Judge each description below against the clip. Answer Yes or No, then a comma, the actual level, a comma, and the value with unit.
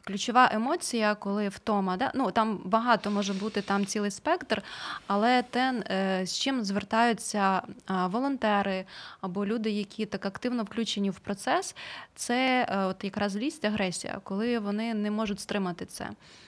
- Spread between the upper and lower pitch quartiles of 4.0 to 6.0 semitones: No, average, 2.9 semitones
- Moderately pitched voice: No, high, 210 Hz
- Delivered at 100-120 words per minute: No, average, 140 wpm